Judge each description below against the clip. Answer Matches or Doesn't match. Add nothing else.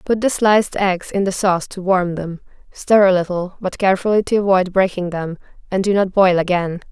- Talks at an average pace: Doesn't match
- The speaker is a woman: Matches